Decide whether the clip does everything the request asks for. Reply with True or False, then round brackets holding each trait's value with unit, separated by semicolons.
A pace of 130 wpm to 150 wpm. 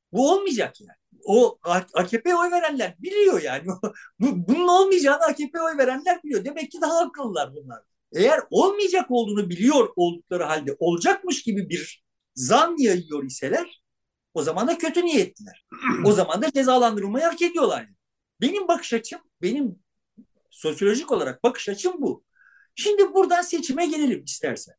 True (140 wpm)